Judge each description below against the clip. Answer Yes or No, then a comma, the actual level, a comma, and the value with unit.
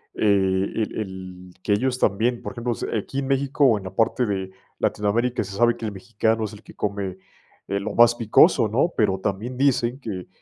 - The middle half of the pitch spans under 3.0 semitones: No, average, 3.4 semitones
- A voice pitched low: Yes, low, 110 Hz